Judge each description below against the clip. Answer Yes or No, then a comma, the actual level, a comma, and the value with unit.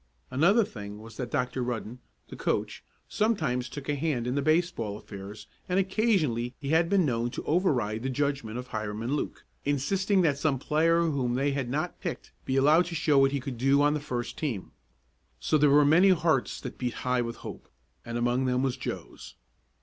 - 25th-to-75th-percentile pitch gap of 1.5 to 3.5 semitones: No, average, 4.4 semitones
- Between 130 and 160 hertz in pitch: Yes, low, 135 Hz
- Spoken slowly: No, fast, 205 wpm